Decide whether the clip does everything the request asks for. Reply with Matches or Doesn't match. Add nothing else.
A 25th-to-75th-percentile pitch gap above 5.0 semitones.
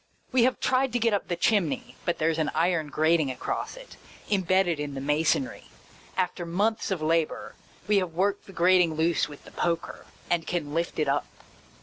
Doesn't match